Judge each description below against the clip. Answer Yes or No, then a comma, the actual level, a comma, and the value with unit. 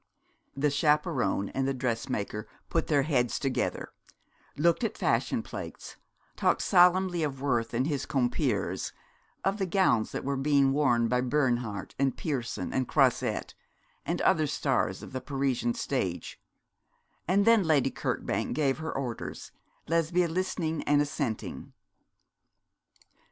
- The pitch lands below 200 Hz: Yes, medium, 140 Hz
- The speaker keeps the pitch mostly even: No, average, 4.2 semitones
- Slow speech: Yes, slow, 130 wpm